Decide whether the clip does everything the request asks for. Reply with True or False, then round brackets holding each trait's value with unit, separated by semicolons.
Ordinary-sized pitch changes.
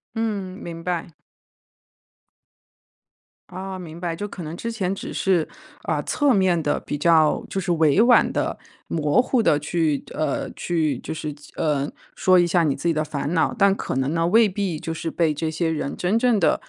True (3.7 semitones)